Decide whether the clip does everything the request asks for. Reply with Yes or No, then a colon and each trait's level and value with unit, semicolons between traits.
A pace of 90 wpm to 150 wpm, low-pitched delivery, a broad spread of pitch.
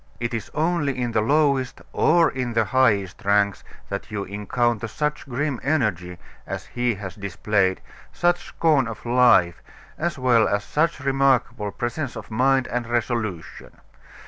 No: average, 145 wpm; low, 120 Hz; average, 4.6 semitones